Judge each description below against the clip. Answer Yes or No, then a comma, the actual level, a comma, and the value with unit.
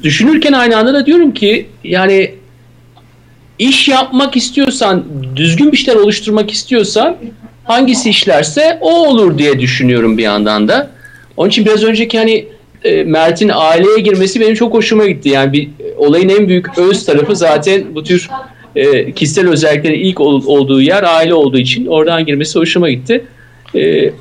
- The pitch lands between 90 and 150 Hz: No, high, 195 Hz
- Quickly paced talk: Yes, fast, 145 wpm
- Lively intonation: Yes, wide, 7.9 semitones